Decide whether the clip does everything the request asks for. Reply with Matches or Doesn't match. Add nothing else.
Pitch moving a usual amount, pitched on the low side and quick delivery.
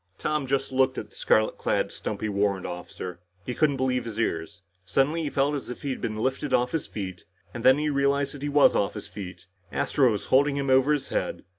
Matches